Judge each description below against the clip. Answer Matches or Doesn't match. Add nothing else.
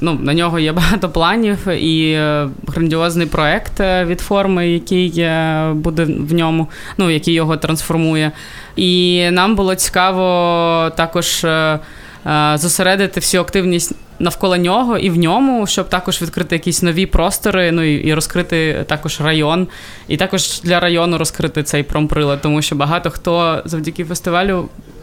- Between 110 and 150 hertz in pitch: Doesn't match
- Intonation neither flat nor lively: Doesn't match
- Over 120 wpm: Matches